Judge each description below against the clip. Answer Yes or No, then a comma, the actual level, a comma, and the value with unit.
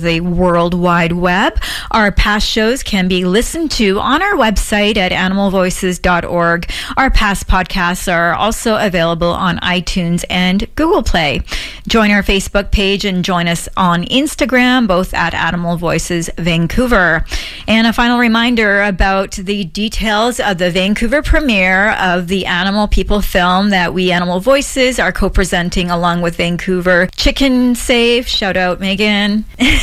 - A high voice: Yes, high, 195 Hz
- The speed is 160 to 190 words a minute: No, average, 145 wpm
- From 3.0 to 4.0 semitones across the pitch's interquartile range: Yes, average, 3.7 semitones